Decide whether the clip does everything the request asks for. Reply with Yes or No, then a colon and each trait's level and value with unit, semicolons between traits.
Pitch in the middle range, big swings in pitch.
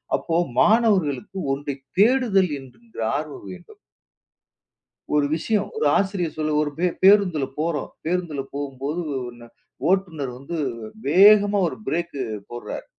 Yes: medium, 165 Hz; wide, 5.7 semitones